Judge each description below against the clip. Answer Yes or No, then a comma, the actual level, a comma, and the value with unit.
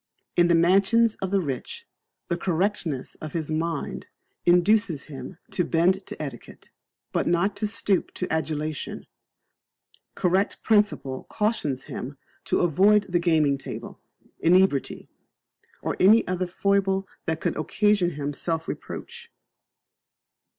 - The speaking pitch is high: No, medium, 175 Hz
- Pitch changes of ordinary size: Yes, average, 4.1 semitones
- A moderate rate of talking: No, slow, 125 wpm